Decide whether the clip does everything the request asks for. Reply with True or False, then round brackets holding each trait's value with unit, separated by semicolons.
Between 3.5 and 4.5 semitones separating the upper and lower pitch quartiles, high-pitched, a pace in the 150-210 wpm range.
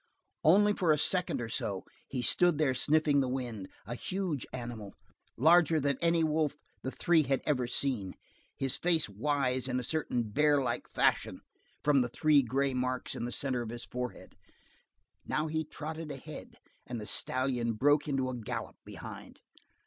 False (3.9 semitones; 135 Hz; 170 wpm)